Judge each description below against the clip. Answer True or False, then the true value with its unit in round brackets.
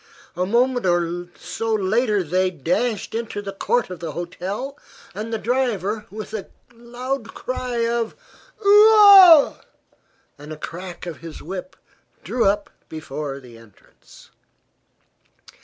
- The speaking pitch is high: True (215 Hz)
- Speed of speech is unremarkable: False (125 wpm)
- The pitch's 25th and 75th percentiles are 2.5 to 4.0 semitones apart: False (5.4 semitones)